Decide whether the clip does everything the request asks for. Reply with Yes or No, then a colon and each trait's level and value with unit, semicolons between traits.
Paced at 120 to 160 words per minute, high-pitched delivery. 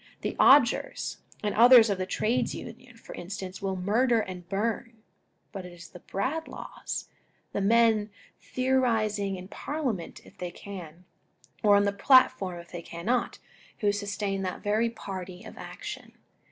Yes: average, 150 wpm; high, 205 Hz